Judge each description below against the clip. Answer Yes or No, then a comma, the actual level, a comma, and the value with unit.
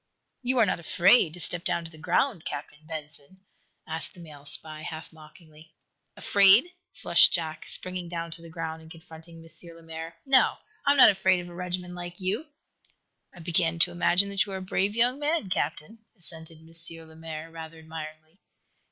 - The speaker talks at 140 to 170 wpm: No, average, 180 wpm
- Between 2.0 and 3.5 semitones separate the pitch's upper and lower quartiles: Yes, narrow, 2.6 semitones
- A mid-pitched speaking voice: Yes, medium, 170 Hz